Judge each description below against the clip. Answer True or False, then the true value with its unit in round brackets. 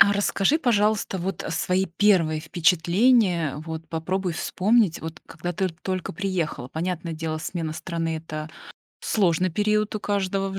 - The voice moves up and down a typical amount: True (3.4 semitones)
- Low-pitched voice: False (180 Hz)